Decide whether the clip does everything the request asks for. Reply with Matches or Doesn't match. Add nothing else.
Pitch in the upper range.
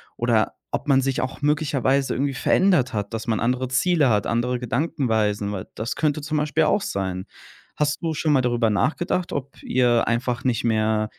Doesn't match